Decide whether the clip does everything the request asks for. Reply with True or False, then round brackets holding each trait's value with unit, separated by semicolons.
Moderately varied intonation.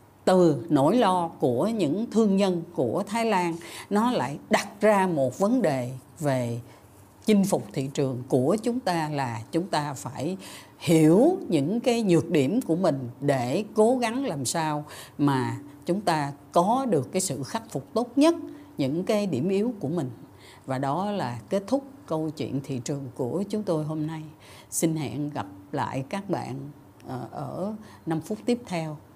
False (6.7 semitones)